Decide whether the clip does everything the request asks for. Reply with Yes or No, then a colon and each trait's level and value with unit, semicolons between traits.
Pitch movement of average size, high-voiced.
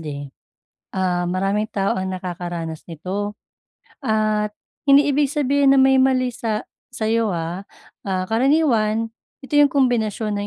No: wide, 6.0 semitones; high, 215 Hz